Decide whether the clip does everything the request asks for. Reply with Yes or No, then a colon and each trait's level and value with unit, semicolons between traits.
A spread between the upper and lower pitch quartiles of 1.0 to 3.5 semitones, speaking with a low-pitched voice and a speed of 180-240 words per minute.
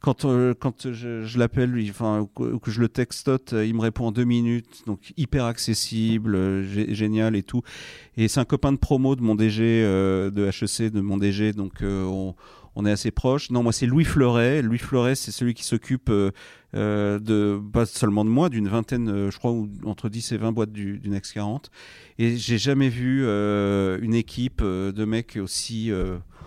Yes: average, 2.9 semitones; low, 110 Hz; average, 200 wpm